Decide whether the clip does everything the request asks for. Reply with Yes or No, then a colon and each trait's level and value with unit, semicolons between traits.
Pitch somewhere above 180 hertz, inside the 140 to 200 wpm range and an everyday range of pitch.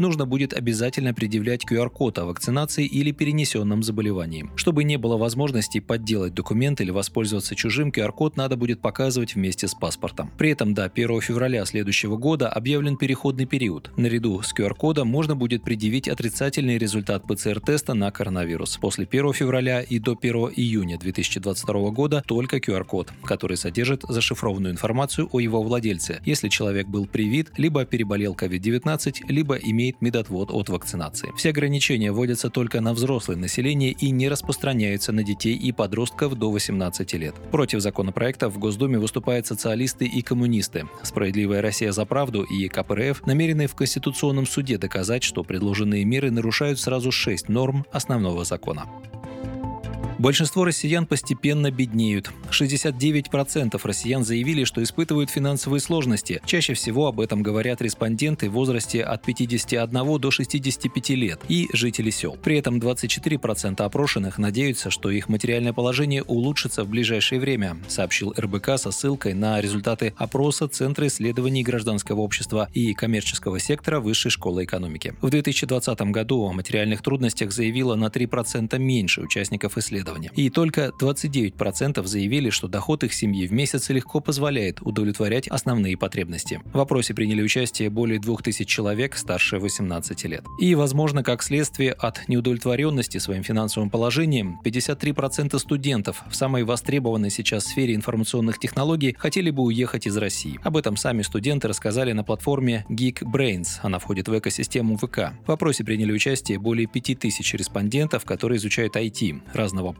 No: low, 120 Hz; average, 145 wpm; average, 4.4 semitones